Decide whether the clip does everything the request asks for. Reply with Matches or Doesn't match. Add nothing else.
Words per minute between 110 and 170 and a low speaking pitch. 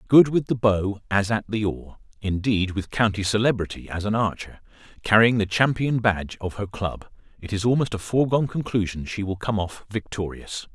Matches